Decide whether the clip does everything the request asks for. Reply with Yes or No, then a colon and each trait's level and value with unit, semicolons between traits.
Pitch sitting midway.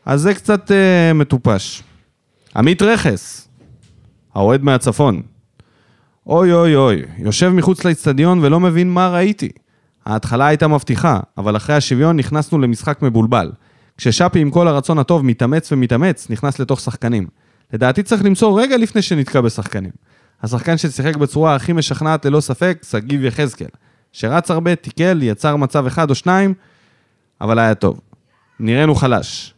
Yes: medium, 145 Hz